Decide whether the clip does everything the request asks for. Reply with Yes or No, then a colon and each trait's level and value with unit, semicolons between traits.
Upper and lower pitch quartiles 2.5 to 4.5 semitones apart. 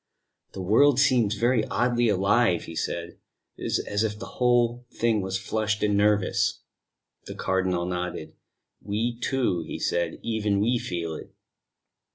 Yes: average, 4.1 semitones